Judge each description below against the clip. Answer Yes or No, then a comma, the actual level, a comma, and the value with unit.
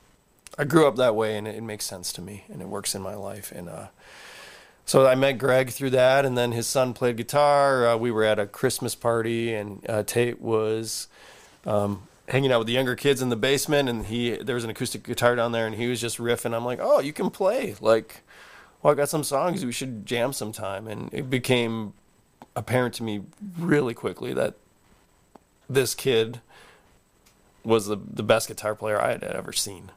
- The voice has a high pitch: No, low, 120 Hz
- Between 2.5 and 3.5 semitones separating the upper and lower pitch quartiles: Yes, average, 2.8 semitones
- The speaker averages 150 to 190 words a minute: No, fast, 205 wpm